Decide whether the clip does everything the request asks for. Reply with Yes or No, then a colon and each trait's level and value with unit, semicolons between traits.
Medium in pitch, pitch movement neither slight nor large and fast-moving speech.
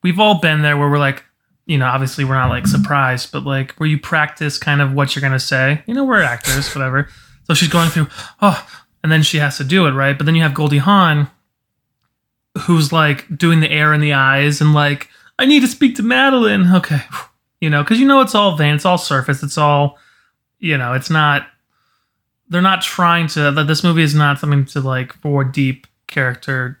Yes: medium, 145 Hz; average, 3.8 semitones; fast, 220 wpm